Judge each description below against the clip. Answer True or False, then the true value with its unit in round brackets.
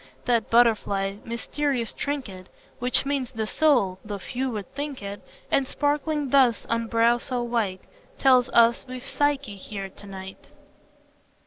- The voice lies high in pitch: True (235 Hz)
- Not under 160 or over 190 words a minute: False (140 wpm)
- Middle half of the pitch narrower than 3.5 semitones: False (4.8 semitones)